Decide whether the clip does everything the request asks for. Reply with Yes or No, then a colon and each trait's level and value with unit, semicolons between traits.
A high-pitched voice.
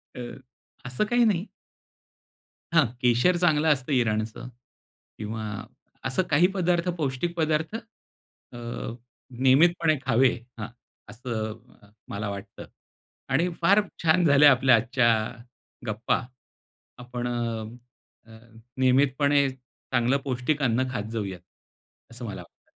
No: low, 130 Hz